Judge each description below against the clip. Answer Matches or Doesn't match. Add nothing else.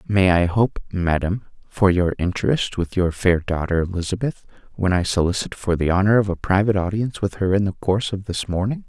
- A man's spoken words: Matches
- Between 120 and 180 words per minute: Doesn't match